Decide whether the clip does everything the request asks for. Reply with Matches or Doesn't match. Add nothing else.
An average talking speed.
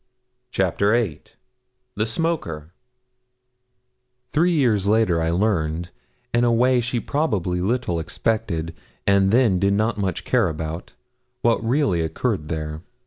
Doesn't match